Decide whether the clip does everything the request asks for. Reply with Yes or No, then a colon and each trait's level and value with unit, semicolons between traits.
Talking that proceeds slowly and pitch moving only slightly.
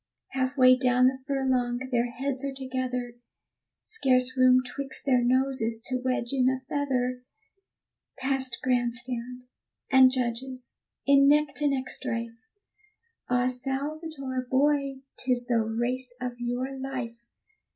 Yes: slow, 130 wpm; narrow, 1.4 semitones